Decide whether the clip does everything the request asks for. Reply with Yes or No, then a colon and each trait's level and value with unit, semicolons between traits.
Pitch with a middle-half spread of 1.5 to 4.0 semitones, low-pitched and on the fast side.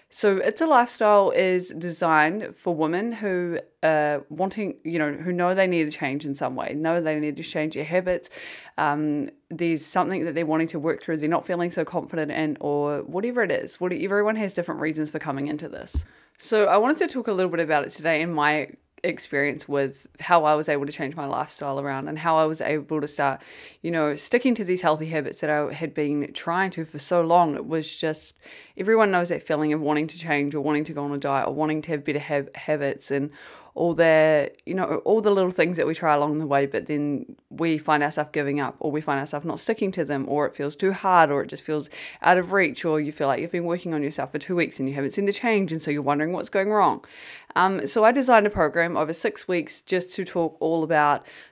No: average, 3.3 semitones; medium, 160 Hz; fast, 245 wpm